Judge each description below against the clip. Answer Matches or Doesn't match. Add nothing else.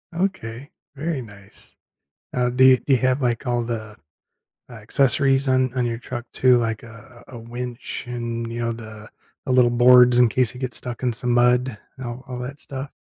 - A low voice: Matches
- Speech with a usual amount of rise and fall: Doesn't match